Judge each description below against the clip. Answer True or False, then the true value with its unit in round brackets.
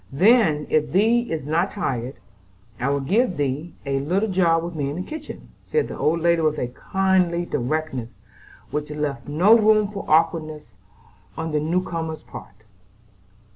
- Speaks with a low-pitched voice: False (160 Hz)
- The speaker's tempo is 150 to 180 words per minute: True (165 wpm)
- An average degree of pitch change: True (4.3 semitones)